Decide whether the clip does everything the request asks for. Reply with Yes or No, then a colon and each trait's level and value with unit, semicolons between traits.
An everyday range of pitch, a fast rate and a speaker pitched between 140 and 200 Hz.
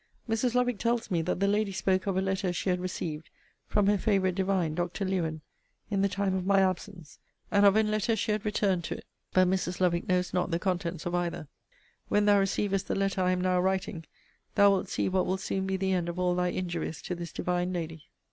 No: narrow, 2.0 semitones; fast, 230 wpm; medium, 185 Hz